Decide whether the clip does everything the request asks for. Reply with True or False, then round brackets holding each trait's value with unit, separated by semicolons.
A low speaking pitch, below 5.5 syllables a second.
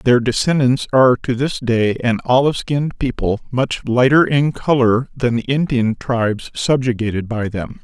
True (125 Hz; 4.7 syllables/s)